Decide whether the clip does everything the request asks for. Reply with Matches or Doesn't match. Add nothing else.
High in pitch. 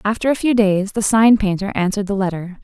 Matches